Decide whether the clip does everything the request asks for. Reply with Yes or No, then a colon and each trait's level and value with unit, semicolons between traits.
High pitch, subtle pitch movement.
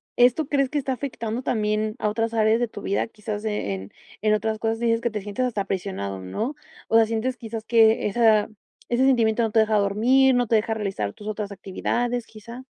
Yes: high, 220 Hz; narrow, 2.3 semitones